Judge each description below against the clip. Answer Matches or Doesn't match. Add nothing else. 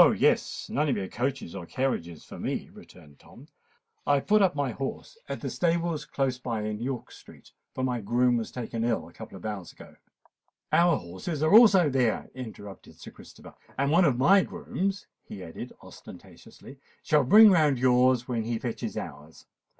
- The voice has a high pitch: Doesn't match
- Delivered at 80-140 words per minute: Doesn't match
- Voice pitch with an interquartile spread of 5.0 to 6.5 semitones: Matches